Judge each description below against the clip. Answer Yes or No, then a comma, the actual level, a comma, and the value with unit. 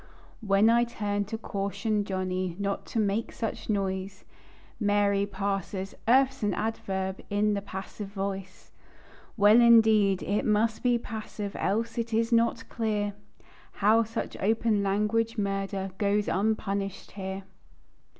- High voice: Yes, high, 205 Hz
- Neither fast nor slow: No, slow, 130 wpm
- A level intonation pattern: Yes, narrow, 2.2 semitones